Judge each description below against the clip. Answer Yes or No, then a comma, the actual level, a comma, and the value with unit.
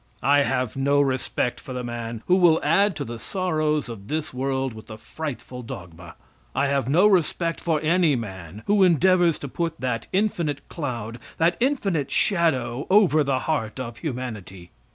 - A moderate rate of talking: Yes, average, 170 wpm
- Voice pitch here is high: No, medium, 140 Hz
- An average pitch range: No, wide, 5.9 semitones